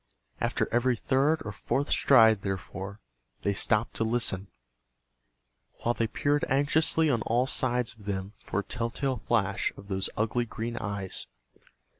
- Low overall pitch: Yes, low, 115 Hz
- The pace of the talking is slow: No, average, 150 wpm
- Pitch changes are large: No, average, 4.1 semitones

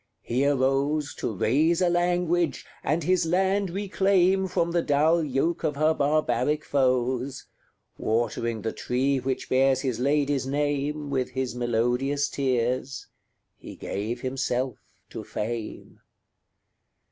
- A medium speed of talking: No, slow, 125 wpm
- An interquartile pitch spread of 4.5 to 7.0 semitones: No, average, 4.1 semitones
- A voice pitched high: No, medium, 140 Hz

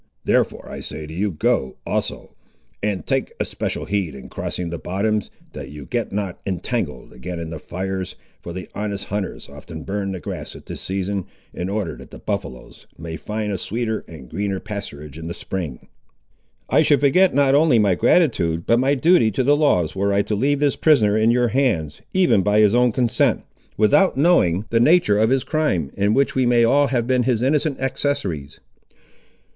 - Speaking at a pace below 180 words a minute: No, average, 195 wpm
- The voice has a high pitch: No, low, 105 Hz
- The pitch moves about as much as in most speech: No, wide, 6.3 semitones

